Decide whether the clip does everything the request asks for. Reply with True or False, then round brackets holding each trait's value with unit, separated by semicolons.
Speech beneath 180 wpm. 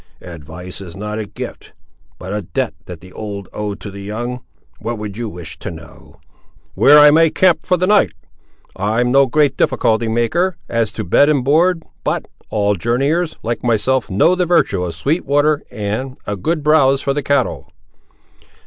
False (185 wpm)